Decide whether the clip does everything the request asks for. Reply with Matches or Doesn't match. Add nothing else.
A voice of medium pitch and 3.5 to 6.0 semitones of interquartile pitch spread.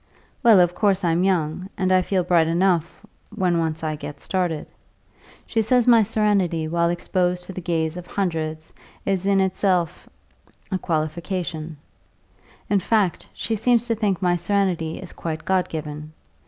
Doesn't match